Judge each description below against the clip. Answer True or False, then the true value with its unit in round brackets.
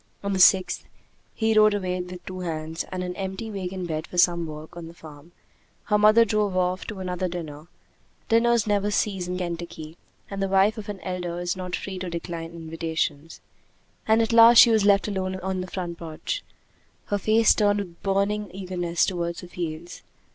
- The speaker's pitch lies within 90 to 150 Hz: False (185 Hz)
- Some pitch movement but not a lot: True (3.0 semitones)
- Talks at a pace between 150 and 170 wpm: False (190 wpm)